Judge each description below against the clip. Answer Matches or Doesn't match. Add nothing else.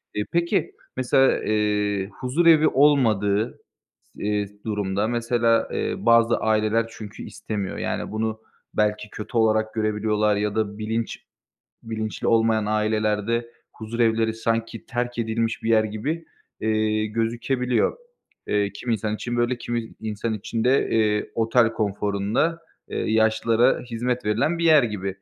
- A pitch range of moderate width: Doesn't match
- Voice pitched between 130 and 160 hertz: Doesn't match